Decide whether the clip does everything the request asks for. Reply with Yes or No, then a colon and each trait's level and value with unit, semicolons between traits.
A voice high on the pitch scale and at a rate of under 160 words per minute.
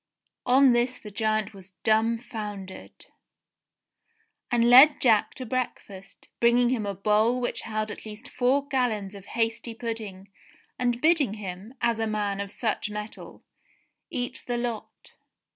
Yes: high, 225 Hz; average, 140 wpm